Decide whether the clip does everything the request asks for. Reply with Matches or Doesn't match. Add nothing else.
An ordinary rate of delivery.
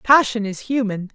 Matches